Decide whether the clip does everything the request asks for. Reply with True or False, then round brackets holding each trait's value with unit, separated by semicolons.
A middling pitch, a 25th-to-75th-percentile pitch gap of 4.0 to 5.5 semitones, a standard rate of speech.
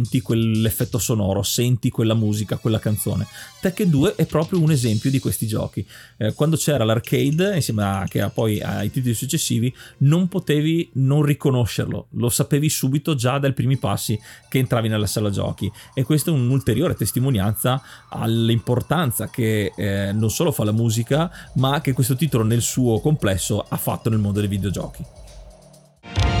False (120 Hz; 4.4 semitones; 155 wpm)